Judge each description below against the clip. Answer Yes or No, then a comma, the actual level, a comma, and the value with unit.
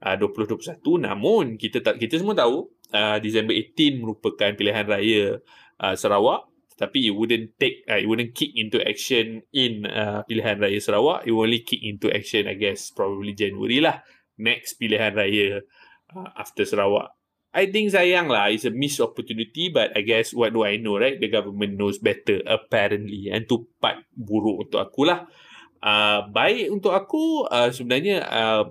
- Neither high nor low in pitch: No, low, 110 Hz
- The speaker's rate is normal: No, fast, 175 wpm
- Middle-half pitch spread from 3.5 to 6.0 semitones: Yes, average, 4.8 semitones